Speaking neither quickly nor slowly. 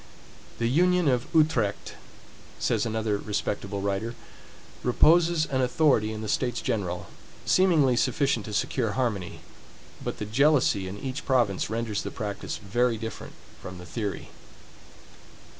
No: slow, 130 wpm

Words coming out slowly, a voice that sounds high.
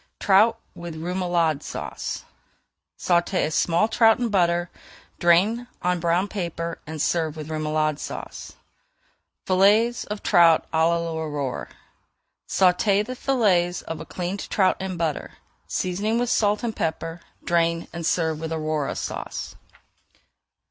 No: slow, 125 wpm; medium, 175 Hz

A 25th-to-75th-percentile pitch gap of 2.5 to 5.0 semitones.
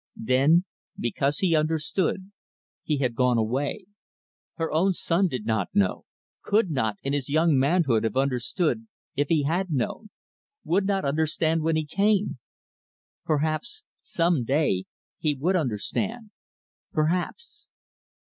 No: wide, 5.4 semitones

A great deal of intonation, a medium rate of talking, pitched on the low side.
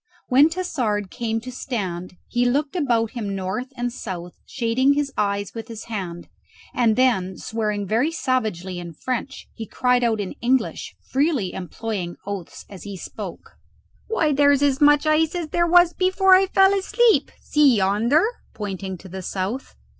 No: wide, 6.2 semitones; average, 165 wpm; high, 235 Hz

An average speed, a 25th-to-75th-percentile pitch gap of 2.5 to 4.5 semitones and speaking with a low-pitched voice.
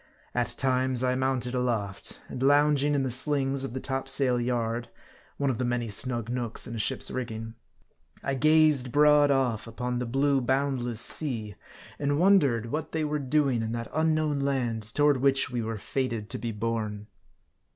Yes: average, 170 wpm; average, 3.2 semitones; low, 130 Hz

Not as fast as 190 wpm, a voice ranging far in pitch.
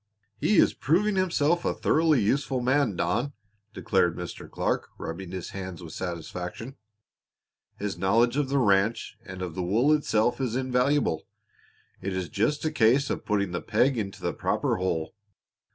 Yes: average, 160 wpm; wide, 6.9 semitones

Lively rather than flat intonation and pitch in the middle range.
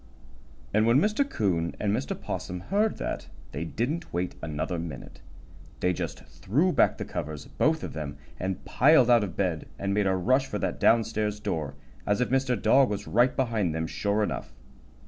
No: wide, 6.6 semitones; low, 105 Hz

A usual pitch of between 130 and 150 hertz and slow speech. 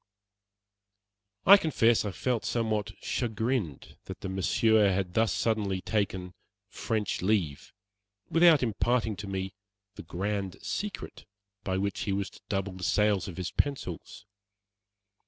No: low, 100 Hz; slow, 130 wpm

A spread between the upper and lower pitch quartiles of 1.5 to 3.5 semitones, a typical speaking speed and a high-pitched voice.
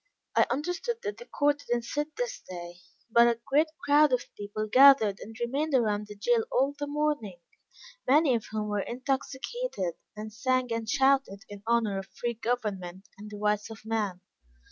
No: average, 5.1 semitones; average, 180 wpm; high, 235 Hz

